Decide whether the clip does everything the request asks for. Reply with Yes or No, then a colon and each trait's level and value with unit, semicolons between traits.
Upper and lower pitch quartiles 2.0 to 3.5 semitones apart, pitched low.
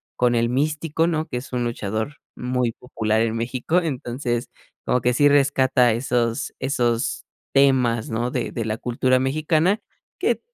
Yes: average, 2.9 semitones; low, 125 Hz